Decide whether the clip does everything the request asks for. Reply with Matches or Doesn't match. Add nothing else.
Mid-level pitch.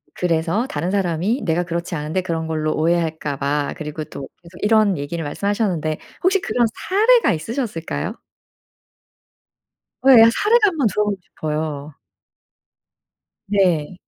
Matches